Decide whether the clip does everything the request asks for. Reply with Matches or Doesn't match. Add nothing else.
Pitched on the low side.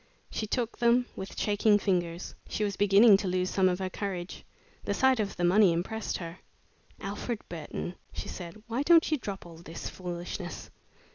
Doesn't match